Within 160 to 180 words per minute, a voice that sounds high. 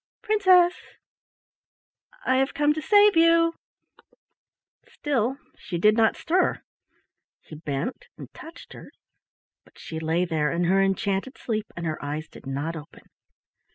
No: slow, 135 wpm; high, 215 Hz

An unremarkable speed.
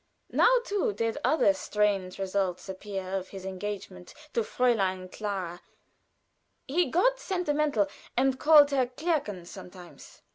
No: slow, 120 wpm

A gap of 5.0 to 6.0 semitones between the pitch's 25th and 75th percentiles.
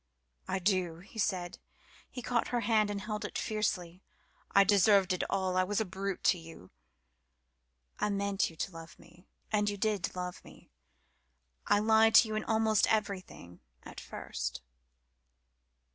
No: average, 3.0 semitones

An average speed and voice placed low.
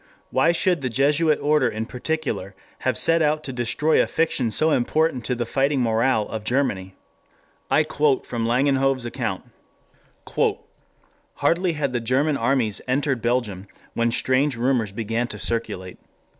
Yes: average, 155 wpm; low, 130 Hz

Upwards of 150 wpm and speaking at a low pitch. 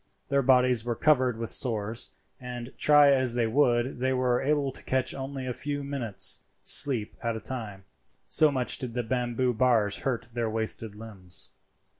Yes: average, 170 wpm; low, 125 Hz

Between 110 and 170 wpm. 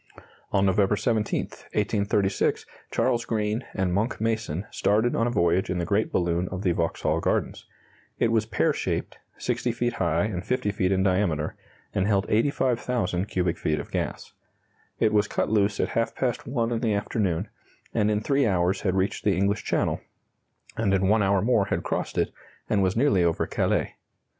No: average, 180 wpm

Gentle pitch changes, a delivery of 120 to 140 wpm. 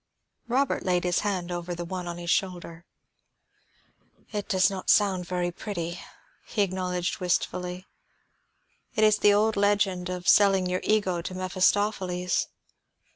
Yes: narrow, 2.3 semitones; slow, 135 wpm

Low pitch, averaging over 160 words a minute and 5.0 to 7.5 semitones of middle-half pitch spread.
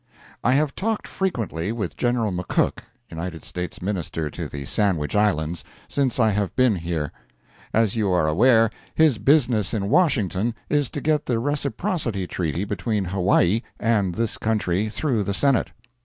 No: low, 105 Hz; average, 155 wpm; wide, 5.6 semitones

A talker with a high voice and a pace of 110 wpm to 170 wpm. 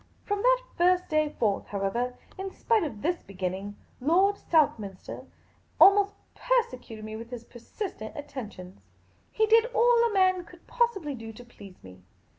Yes: very high, 295 Hz; average, 160 wpm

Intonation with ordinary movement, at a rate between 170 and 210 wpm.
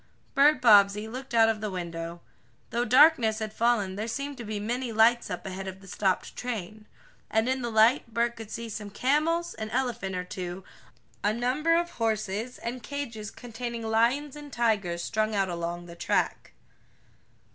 Yes: average, 3.4 semitones; average, 175 wpm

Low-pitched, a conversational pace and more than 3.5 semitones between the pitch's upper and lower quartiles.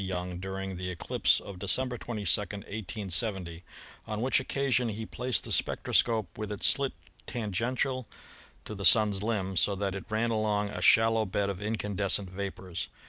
No: low, 105 Hz; average, 160 wpm; average, 2.7 semitones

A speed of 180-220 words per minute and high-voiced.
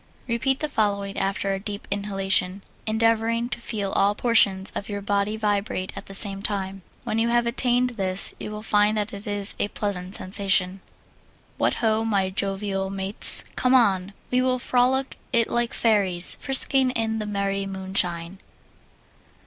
No: average, 160 wpm; high, 205 Hz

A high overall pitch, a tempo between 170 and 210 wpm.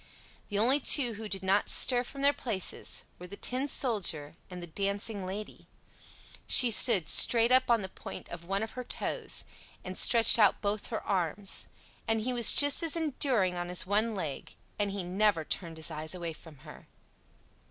Yes: high, 205 Hz; average, 185 wpm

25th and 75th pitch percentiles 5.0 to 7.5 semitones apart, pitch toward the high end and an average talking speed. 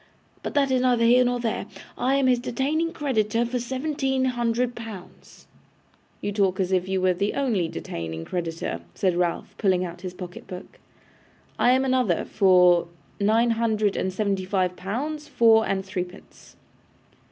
Yes: wide, 5.4 semitones; high, 215 Hz; average, 160 wpm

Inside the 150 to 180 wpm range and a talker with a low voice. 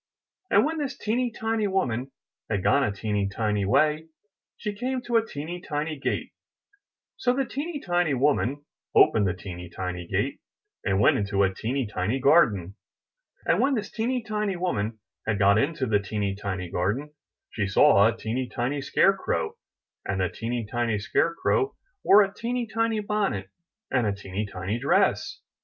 Yes: average, 170 wpm; low, 130 Hz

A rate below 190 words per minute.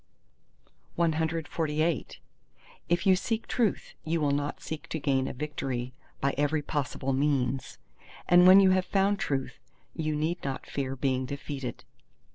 Yes: average, 140 wpm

